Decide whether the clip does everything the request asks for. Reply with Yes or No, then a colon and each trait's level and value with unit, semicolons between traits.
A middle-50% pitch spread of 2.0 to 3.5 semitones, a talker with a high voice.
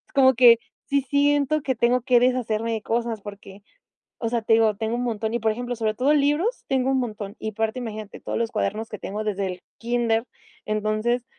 Yes: average, 2.8 semitones; high, 230 Hz